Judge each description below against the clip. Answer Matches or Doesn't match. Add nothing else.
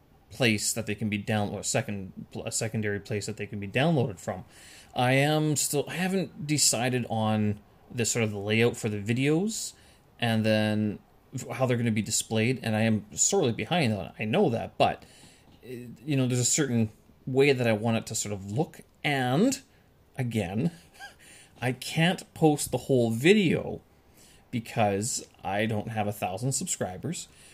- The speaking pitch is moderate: Doesn't match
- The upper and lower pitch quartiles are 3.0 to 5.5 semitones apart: Matches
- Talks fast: Doesn't match